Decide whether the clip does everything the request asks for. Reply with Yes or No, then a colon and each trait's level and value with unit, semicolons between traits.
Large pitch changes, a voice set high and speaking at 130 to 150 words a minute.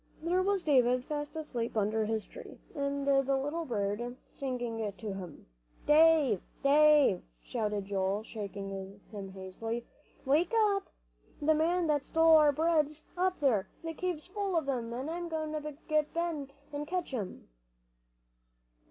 Yes: wide, 6.2 semitones; very high, 280 Hz; average, 145 wpm